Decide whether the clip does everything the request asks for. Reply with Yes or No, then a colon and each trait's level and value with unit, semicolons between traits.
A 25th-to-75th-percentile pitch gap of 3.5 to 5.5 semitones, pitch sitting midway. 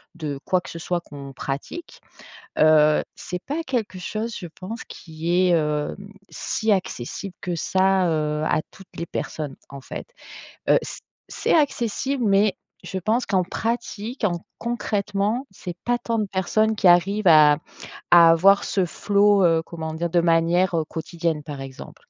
Yes: average, 4.5 semitones; medium, 180 Hz